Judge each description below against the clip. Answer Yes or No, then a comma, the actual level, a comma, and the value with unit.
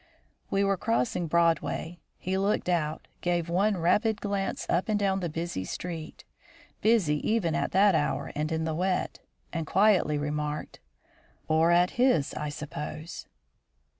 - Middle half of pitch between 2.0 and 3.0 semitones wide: No, average, 3.8 semitones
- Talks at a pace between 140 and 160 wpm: Yes, average, 145 wpm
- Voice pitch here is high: No, medium, 175 Hz